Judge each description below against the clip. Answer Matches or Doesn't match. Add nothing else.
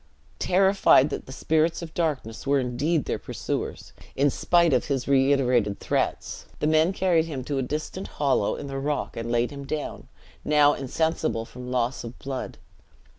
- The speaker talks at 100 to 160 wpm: Doesn't match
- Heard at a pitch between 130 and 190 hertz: Matches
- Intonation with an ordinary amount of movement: Matches